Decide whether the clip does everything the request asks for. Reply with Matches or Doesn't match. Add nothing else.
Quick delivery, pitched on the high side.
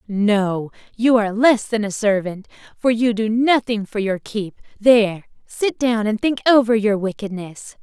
Doesn't match